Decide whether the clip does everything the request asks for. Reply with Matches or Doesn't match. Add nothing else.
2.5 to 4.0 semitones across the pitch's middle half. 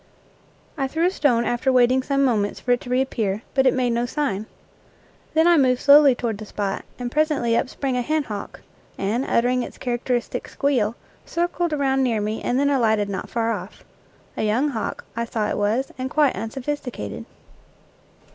Matches